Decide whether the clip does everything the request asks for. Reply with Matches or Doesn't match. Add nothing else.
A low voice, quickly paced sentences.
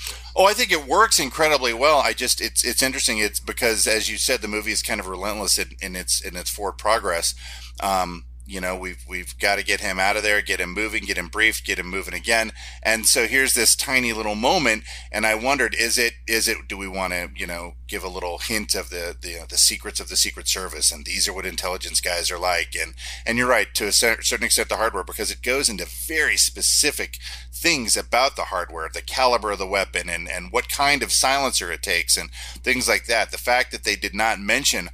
Matches